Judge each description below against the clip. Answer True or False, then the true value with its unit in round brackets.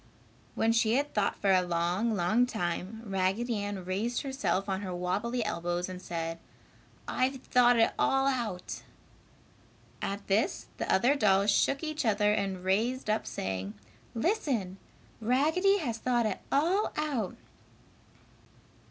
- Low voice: False (215 Hz)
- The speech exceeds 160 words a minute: False (135 wpm)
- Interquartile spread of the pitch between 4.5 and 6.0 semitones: True (5.2 semitones)